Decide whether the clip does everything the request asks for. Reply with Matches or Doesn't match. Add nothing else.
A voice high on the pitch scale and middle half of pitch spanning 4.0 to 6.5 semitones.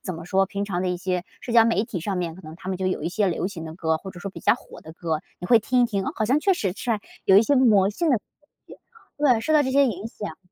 Matches